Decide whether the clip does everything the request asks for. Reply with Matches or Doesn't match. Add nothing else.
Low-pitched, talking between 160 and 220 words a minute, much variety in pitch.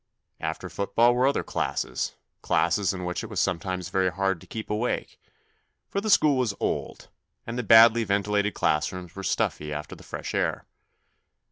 Doesn't match